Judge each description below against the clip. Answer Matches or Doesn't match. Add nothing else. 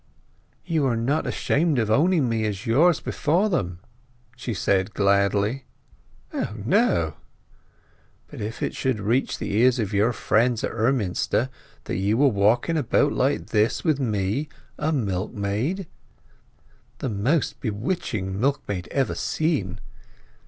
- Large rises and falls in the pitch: Matches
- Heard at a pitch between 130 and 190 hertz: Doesn't match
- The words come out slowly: Matches